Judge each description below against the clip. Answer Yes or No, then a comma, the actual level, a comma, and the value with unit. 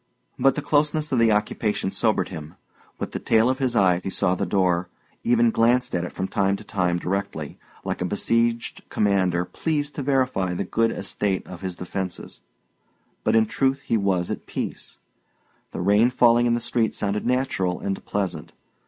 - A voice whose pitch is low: Yes, low, 105 Hz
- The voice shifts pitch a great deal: No, average, 4.6 semitones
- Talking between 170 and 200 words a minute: Yes, average, 180 wpm